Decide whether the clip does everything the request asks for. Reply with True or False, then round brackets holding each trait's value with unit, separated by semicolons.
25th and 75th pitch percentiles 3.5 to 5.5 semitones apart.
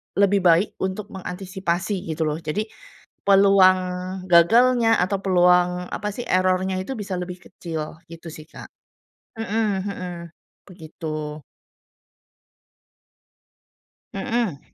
False (2.7 semitones)